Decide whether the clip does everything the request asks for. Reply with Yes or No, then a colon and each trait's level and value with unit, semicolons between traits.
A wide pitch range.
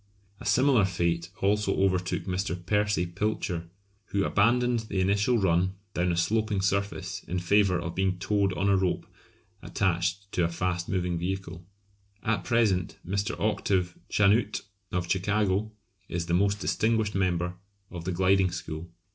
No: narrow, 2.6 semitones